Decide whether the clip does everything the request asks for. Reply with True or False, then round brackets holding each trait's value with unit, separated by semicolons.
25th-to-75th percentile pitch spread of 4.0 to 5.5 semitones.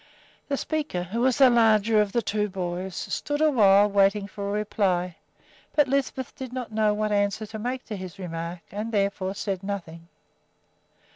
False (3.3 semitones)